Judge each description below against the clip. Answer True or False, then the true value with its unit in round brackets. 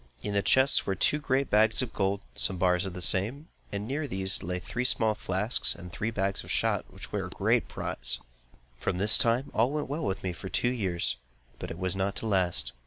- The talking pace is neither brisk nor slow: False (230 wpm)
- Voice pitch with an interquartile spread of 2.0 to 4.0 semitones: False (4.8 semitones)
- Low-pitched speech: True (100 Hz)